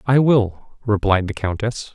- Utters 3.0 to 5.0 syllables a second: Yes, 4.0 syllables/s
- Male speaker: Yes, male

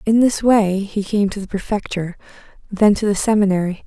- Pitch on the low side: No, high, 200 Hz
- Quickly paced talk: No, average, 185 wpm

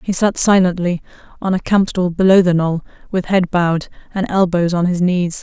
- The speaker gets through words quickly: No, average, 190 wpm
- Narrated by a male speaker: No, female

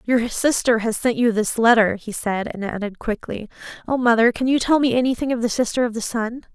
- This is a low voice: No, high, 230 Hz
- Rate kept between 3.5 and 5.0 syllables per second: No, 5.5 syllables/s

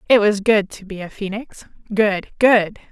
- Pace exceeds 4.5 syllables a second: No, 4.3 syllables/s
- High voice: Yes, high, 205 Hz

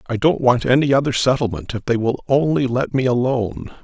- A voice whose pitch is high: No, low, 125 Hz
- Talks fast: No, average, 190 wpm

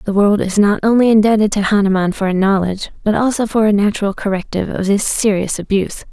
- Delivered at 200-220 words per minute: Yes, fast, 205 wpm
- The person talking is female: Yes, female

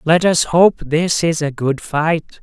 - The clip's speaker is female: No, male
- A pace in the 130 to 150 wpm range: No, average, 200 wpm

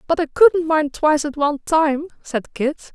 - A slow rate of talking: No, fast, 205 wpm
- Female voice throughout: Yes, female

